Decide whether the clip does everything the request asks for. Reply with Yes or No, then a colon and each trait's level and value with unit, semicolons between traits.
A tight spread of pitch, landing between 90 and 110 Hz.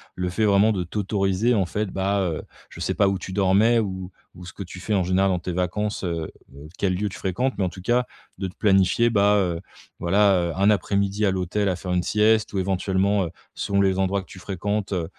Yes: narrow, 2.1 semitones; very low, 95 Hz